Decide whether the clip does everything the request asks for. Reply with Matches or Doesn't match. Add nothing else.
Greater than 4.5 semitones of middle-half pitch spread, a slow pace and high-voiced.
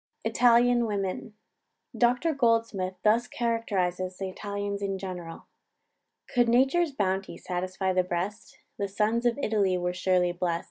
Doesn't match